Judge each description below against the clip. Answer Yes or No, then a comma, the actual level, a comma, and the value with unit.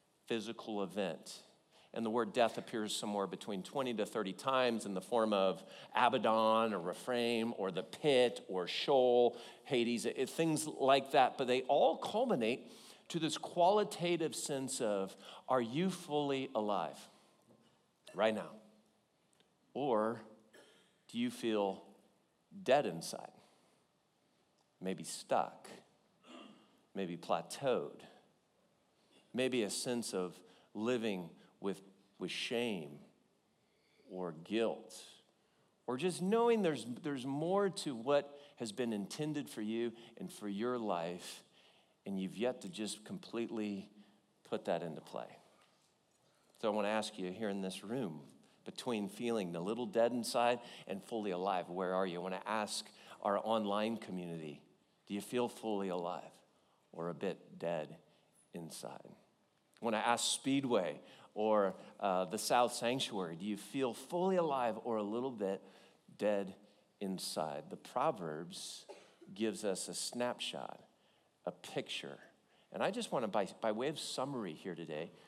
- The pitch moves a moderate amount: Yes, average, 4.7 semitones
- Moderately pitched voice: No, low, 110 Hz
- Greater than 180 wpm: No, slow, 135 wpm